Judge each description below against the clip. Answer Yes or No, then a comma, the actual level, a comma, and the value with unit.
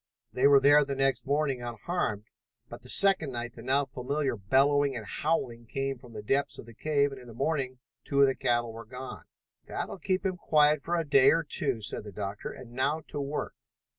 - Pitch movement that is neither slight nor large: Yes, average, 3.4 semitones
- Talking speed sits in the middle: No, fast, 220 wpm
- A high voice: No, low, 135 Hz